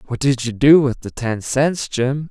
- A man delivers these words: Yes, male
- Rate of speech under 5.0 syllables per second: Yes, 4.2 syllables/s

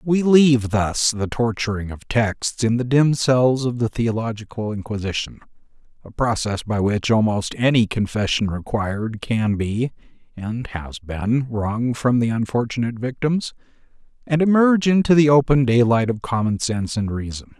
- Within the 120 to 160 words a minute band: Yes, average, 150 wpm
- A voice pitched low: Yes, low, 120 Hz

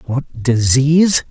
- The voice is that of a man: Yes, male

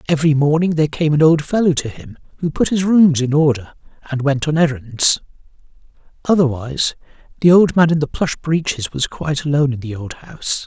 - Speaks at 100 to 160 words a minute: No, average, 190 wpm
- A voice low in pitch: No, medium, 150 Hz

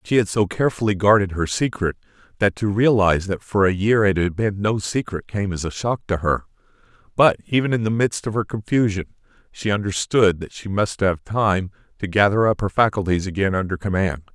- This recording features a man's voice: Yes, male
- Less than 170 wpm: No, average, 200 wpm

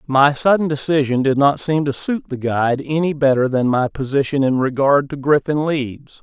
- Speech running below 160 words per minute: No, average, 195 wpm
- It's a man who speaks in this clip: Yes, male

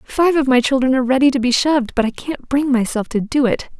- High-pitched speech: Yes, very high, 260 Hz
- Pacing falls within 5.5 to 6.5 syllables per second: Yes, 6.1 syllables/s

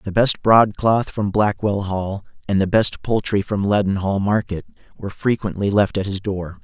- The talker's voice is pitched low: Yes, low, 100 Hz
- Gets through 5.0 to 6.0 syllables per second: No, 4.7 syllables/s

